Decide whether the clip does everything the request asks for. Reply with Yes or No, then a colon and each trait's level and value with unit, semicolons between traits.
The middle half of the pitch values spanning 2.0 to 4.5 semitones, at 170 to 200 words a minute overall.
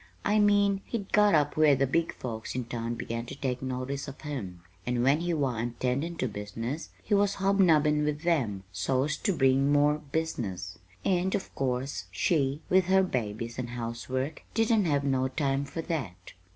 No: average, 5.2 semitones; average, 180 wpm